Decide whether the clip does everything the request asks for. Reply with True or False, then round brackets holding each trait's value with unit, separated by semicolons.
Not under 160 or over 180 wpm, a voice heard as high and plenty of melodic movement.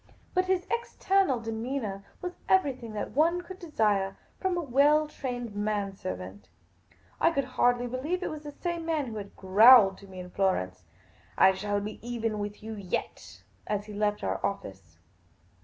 True (175 wpm; 225 Hz; 7.1 semitones)